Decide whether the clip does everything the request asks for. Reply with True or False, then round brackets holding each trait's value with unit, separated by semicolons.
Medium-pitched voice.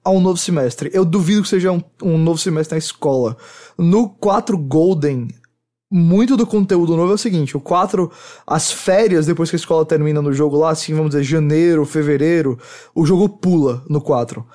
True (165 Hz)